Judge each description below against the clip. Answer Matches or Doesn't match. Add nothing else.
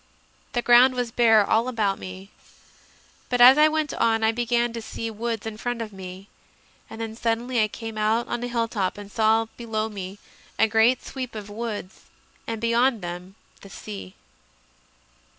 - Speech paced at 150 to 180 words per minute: Matches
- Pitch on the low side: Doesn't match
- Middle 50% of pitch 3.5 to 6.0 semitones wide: Doesn't match